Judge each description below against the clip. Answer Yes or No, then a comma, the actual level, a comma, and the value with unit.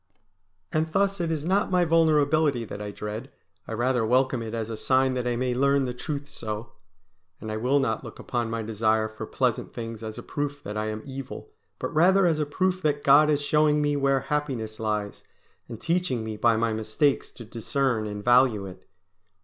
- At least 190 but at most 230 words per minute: Yes, fast, 205 wpm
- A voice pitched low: Yes, low, 130 Hz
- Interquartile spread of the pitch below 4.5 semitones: No, average, 5.0 semitones